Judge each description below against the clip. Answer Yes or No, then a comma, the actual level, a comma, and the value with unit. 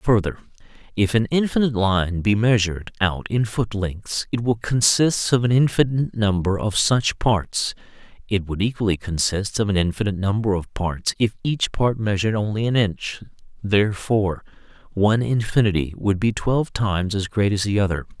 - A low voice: Yes, low, 105 Hz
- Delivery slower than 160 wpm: No, average, 165 wpm